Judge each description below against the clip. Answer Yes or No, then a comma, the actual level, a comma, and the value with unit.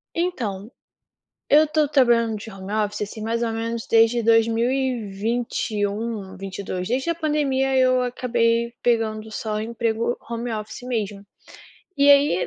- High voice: Yes, high, 230 Hz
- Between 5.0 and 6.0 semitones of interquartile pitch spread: No, average, 2.7 semitones